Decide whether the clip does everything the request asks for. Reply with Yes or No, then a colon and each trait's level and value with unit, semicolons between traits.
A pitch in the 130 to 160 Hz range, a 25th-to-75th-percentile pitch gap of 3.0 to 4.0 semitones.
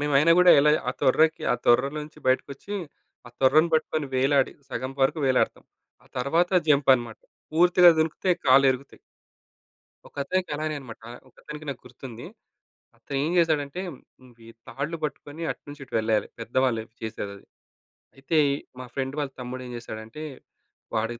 Yes: medium, 140 Hz; average, 3.5 semitones